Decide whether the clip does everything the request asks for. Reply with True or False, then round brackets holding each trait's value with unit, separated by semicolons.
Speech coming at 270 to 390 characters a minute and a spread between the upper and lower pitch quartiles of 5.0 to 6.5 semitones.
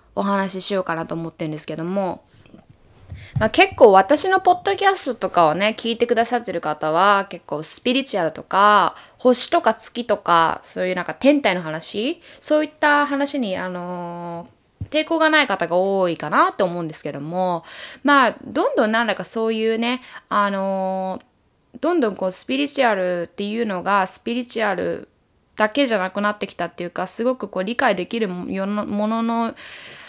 True (355 characters per minute; 5.5 semitones)